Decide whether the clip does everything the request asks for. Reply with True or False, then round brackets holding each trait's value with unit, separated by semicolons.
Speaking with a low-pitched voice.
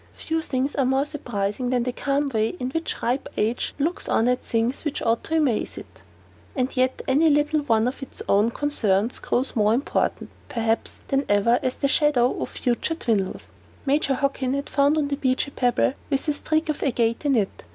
False (260 Hz)